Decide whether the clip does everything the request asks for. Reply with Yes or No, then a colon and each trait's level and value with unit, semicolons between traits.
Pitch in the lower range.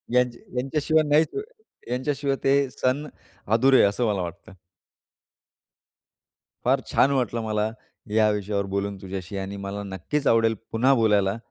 Yes: low, 115 Hz